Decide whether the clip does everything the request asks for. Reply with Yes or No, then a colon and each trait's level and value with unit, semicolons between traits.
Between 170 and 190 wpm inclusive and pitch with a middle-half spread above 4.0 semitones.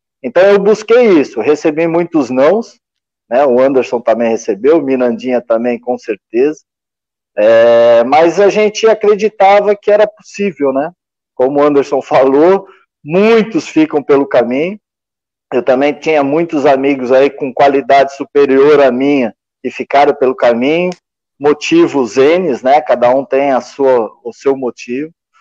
No: average, 140 wpm; wide, 5.5 semitones